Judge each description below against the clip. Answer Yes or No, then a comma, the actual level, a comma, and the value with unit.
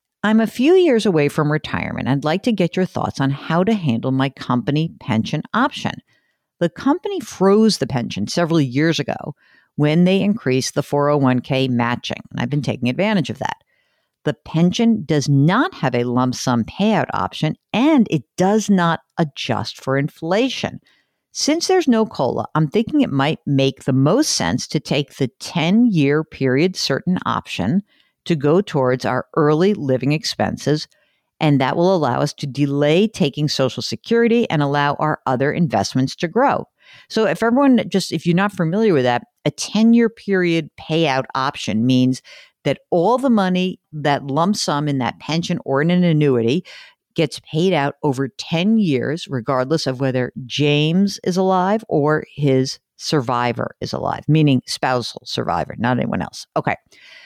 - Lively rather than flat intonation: Yes, wide, 6.3 semitones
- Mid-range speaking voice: Yes, medium, 155 Hz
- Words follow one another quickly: No, average, 165 wpm